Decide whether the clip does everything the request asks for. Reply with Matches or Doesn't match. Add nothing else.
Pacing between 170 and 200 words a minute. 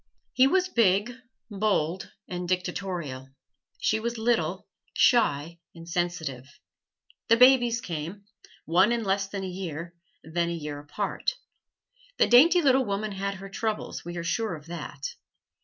Doesn't match